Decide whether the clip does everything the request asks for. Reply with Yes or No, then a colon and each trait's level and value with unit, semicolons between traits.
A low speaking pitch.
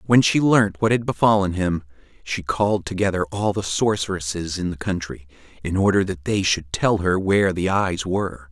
Yes: very low, 95 Hz